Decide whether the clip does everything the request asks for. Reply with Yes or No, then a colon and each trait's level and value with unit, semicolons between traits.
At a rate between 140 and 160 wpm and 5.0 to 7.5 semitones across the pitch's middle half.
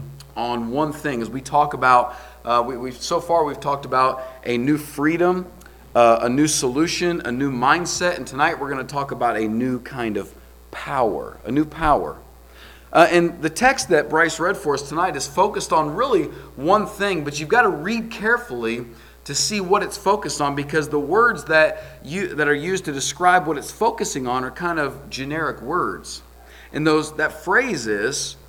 No: average, 195 wpm; wide, 5.5 semitones